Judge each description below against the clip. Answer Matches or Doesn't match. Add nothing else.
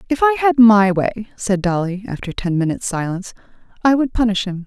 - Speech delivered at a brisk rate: Doesn't match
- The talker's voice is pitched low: Doesn't match